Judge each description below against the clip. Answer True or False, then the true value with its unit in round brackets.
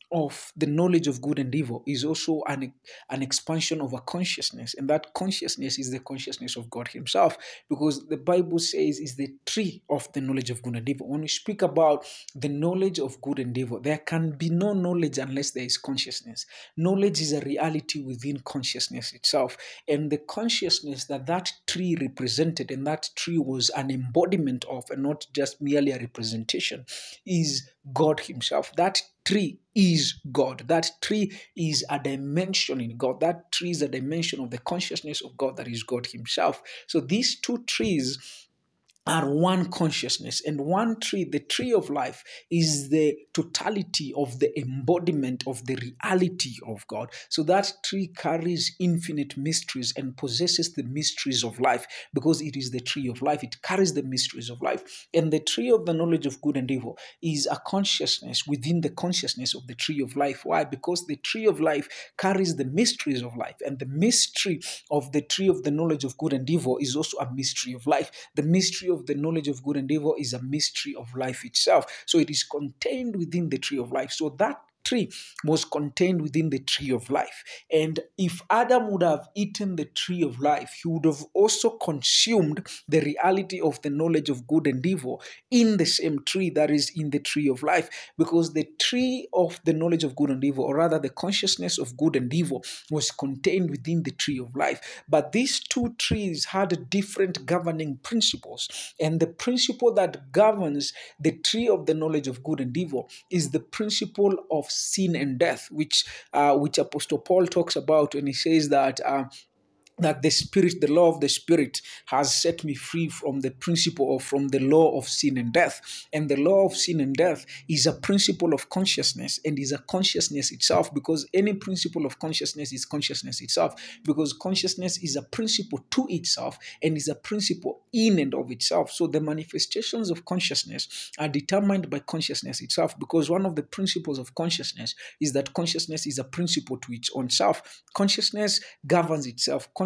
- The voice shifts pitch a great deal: False (4.1 semitones)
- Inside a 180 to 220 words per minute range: True (190 wpm)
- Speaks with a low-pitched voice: False (155 Hz)